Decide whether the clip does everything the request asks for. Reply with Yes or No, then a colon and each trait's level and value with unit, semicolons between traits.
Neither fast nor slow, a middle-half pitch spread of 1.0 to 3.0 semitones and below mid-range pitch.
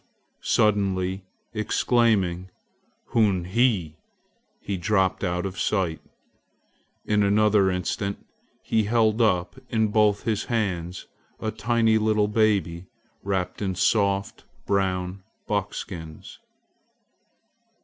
No: slow, 90 wpm; average, 2.7 semitones; low, 100 Hz